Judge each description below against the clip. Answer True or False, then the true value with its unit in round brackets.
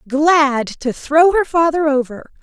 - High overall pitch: True (295 Hz)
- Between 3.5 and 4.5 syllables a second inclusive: True (3.6 syllables/s)